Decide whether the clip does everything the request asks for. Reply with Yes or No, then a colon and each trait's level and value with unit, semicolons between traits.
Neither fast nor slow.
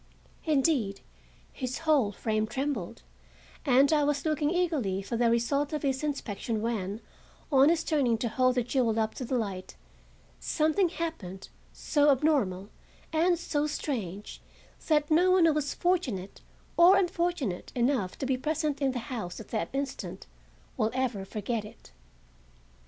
Yes: average, 150 wpm